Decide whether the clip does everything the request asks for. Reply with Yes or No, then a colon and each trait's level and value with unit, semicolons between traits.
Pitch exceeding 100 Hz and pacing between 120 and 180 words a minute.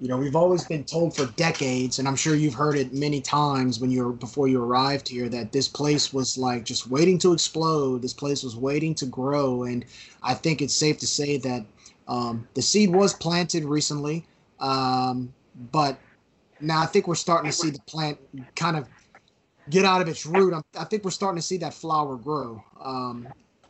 No: medium, 140 Hz; average, 200 wpm